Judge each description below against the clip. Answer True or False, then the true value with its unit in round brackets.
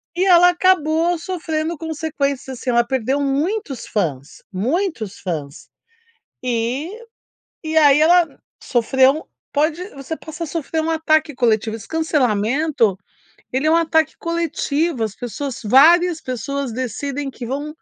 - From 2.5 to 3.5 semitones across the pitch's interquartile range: False (4.6 semitones)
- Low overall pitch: False (285 Hz)